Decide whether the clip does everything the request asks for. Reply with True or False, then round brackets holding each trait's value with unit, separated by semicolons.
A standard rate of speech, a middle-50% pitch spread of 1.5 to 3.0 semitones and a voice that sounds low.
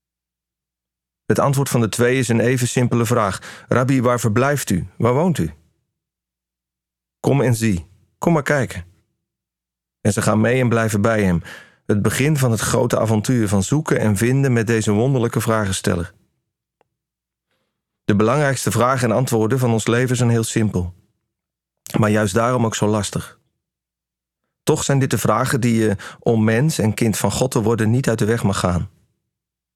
False (165 wpm; 4.2 semitones; 110 Hz)